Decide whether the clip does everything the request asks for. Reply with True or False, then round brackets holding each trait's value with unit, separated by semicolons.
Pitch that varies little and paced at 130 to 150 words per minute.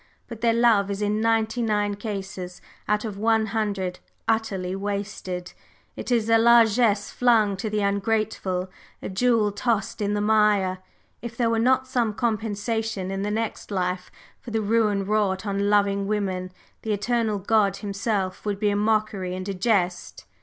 False (2.2 semitones; 165 wpm)